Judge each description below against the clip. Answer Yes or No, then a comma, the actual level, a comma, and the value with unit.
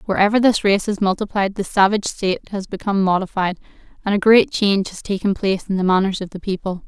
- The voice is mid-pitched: No, high, 200 Hz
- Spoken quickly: Yes, fast, 210 wpm